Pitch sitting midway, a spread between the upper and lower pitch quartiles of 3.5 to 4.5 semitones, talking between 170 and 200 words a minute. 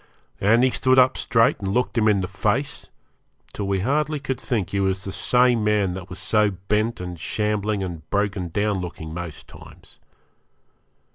No: low, 105 Hz; average, 3.8 semitones; average, 180 wpm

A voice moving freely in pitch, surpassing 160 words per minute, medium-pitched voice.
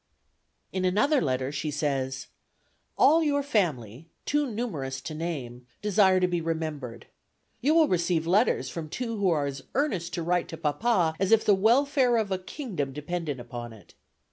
Yes: wide, 7.3 semitones; average, 170 wpm; medium, 170 Hz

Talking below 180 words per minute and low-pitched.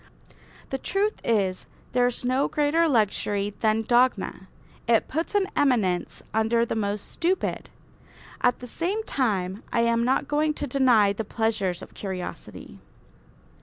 No: average, 140 wpm; high, 235 Hz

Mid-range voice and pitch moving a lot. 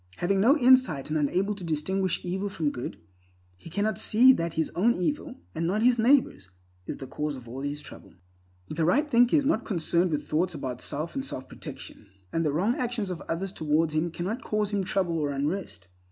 Yes: medium, 175 Hz; wide, 6.1 semitones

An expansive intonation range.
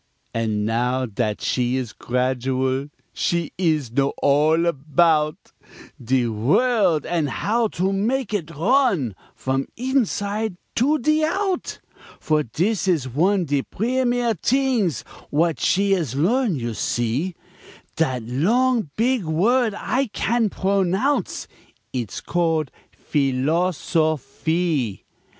Yes: wide, 8.7 semitones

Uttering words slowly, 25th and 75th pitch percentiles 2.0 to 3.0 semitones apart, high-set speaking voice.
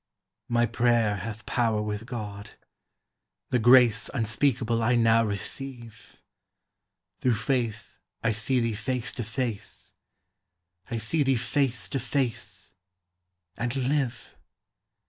No: slow, 110 wpm; narrow, 2.4 semitones; low, 115 Hz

